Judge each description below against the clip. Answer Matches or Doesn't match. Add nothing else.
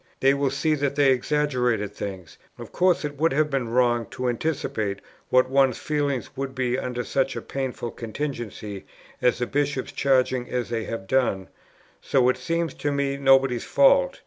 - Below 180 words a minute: Matches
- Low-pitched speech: Matches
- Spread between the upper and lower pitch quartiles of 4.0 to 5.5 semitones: Doesn't match